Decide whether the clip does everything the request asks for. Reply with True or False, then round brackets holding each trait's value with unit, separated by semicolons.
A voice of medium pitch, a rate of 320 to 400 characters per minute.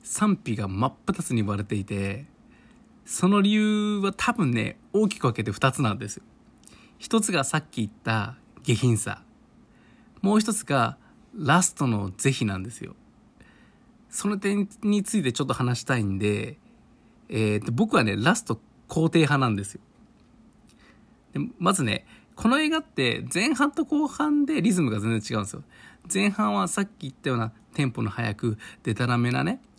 False (145 Hz; 290 characters per minute)